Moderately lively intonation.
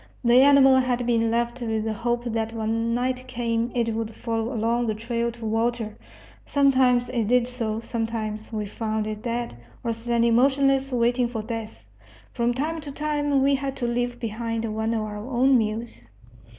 No: narrow, 2.0 semitones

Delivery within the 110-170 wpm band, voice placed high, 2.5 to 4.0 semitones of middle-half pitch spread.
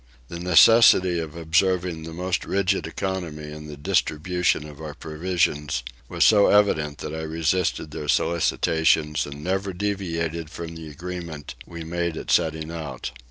No: average, 150 wpm; very low, 80 Hz; average, 2.8 semitones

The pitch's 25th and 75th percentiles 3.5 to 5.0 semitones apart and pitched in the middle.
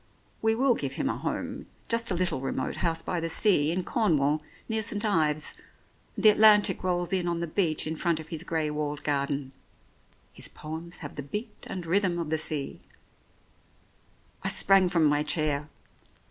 Yes: average, 4.4 semitones; medium, 165 Hz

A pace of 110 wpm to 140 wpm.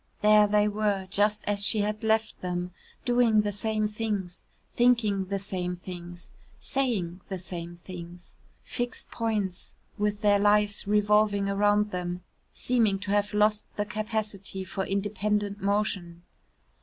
Yes: slow, 135 wpm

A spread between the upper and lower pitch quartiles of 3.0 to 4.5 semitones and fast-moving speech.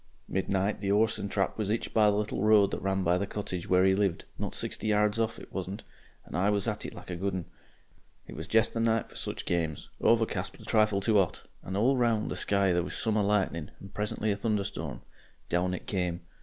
No: narrow, 2.4 semitones; fast, 235 wpm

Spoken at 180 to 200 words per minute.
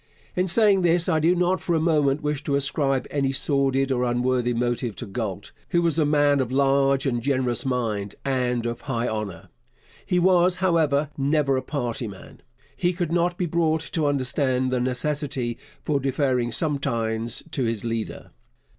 No: average, 170 wpm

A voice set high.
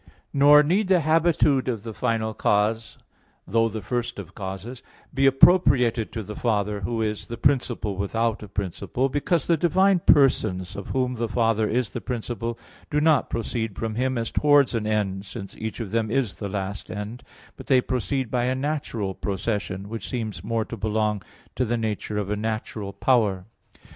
No: low, 115 Hz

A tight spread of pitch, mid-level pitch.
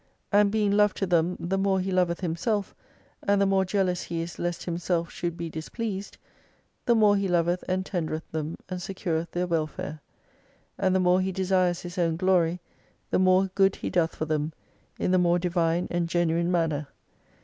Yes: narrow, 2.2 semitones; medium, 180 Hz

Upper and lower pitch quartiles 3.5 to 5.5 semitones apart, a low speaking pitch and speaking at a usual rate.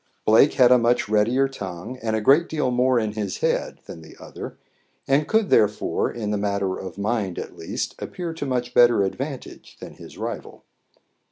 Yes: average, 4.4 semitones; low, 120 Hz; average, 185 wpm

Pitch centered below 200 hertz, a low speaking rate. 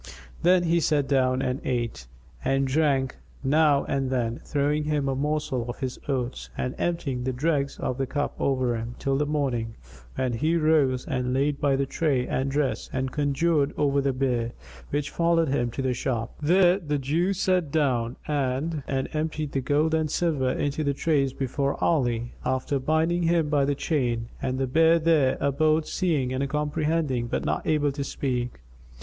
No: medium, 140 Hz; average, 180 wpm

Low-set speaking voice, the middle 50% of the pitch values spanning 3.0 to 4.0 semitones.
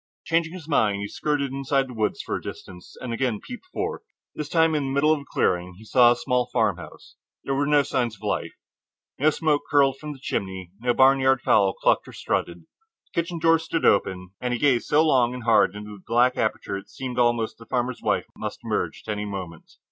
No: low, 125 Hz; wide, 5.4 semitones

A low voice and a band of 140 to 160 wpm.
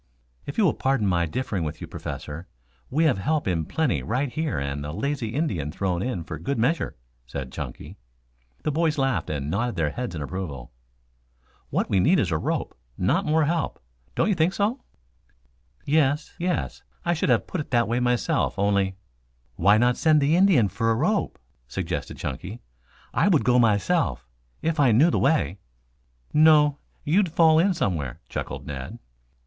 No: low, 125 Hz; average, 175 wpm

